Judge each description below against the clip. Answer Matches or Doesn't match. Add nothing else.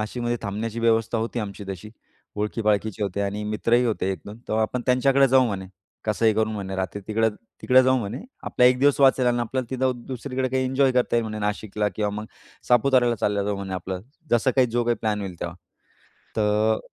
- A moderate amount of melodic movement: Matches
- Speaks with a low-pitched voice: Matches